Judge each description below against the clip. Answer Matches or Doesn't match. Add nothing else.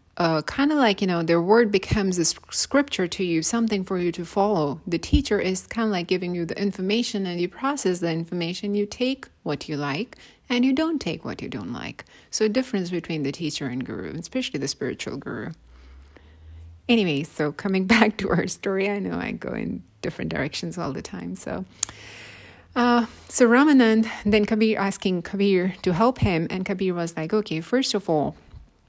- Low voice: Doesn't match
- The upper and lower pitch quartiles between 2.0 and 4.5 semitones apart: Doesn't match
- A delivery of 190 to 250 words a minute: Matches